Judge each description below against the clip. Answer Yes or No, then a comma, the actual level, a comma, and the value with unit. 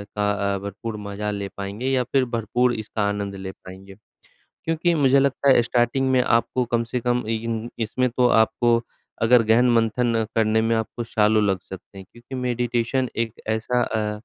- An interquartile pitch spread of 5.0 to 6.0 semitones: No, average, 2.8 semitones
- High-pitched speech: No, low, 115 Hz